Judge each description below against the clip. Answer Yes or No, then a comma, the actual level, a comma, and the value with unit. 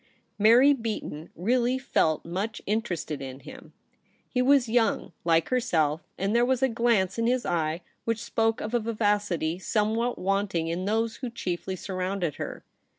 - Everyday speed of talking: Yes, average, 170 wpm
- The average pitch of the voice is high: Yes, high, 215 Hz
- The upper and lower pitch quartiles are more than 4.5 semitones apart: Yes, average, 5.1 semitones